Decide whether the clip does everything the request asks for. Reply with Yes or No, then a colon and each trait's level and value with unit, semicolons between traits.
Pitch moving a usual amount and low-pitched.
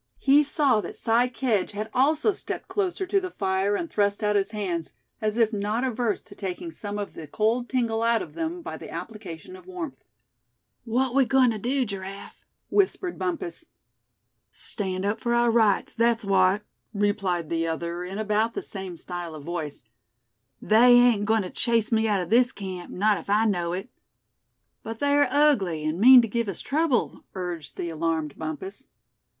No: average, 4.7 semitones; high, 215 Hz